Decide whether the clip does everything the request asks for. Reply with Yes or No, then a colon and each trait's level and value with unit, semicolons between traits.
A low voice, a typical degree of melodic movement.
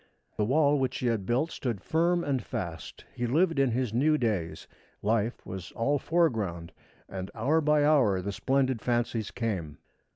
No: low, 120 Hz; wide, 6.1 semitones